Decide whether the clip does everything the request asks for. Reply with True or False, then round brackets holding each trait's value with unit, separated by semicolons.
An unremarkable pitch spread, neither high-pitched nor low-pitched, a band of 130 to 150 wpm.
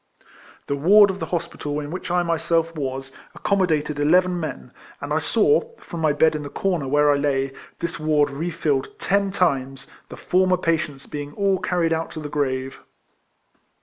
False (3.8 semitones; 160 Hz; 180 wpm)